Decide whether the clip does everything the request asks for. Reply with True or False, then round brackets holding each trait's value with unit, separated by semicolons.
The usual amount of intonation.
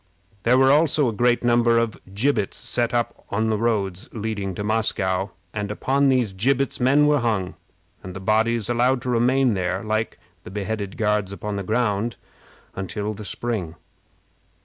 True (3.3 semitones)